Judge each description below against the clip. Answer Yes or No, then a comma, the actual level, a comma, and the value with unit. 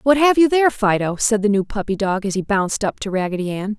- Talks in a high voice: Yes, high, 215 Hz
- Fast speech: Yes, fast, 270 wpm